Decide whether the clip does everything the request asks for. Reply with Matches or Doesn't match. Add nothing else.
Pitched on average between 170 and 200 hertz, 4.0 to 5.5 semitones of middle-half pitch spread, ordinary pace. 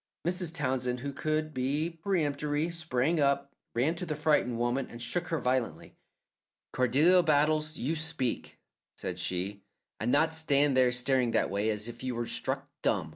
Doesn't match